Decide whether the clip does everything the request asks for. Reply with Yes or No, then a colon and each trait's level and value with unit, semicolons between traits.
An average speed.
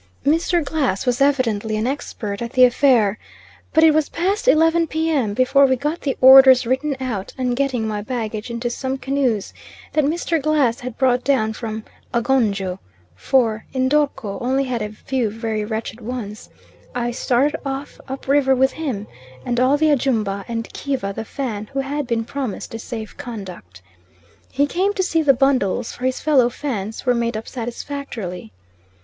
Yes: average, 170 wpm